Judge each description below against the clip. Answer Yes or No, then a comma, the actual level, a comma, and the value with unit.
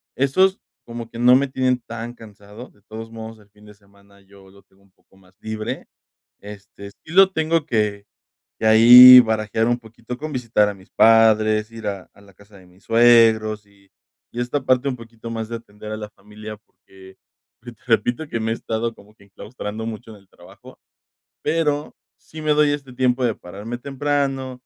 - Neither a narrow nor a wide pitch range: Yes, average, 3.2 semitones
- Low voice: Yes, low, 115 Hz